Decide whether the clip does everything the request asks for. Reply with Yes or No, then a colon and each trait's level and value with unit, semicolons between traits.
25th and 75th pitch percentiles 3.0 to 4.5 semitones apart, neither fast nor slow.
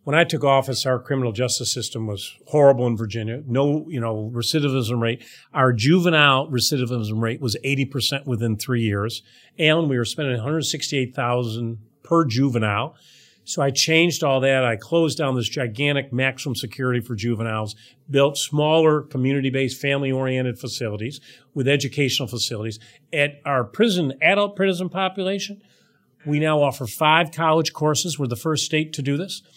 Yes: average, 3.8 semitones; average, 150 wpm